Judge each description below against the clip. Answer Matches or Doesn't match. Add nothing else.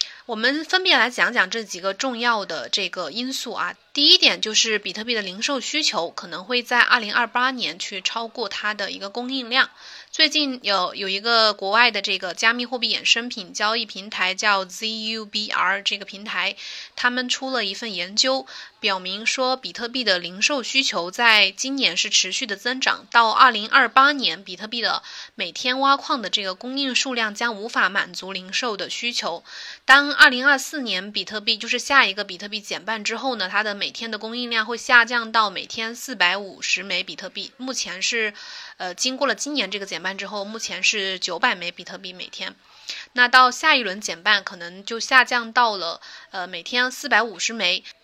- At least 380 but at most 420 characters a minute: Doesn't match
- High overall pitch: Matches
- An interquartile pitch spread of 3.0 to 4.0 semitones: Doesn't match